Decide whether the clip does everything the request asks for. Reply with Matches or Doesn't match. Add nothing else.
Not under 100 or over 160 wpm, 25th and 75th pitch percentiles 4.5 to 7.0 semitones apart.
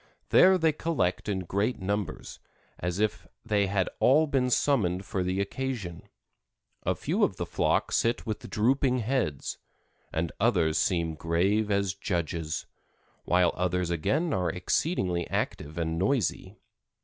Matches